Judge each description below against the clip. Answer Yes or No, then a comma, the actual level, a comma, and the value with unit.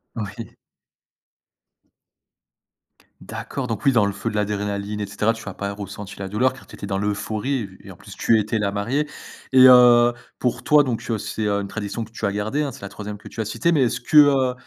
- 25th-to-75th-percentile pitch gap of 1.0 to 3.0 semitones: No, average, 3.5 semitones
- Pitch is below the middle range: Yes, low, 110 Hz